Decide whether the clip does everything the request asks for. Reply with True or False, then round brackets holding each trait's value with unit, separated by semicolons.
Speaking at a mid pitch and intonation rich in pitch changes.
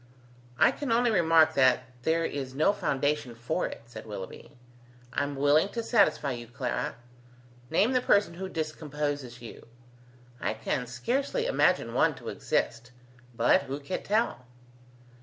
True (145 Hz; 7.0 semitones)